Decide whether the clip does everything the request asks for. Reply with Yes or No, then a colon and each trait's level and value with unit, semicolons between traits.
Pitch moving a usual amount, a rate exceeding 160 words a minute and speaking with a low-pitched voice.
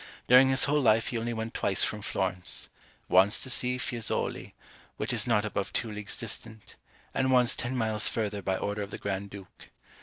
Yes: average, 3.2 semitones; average, 190 wpm; low, 110 Hz